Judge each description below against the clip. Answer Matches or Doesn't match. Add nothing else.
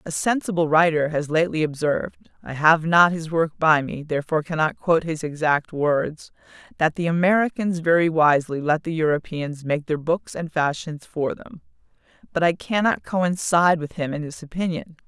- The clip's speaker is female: Matches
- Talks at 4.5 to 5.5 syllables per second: Doesn't match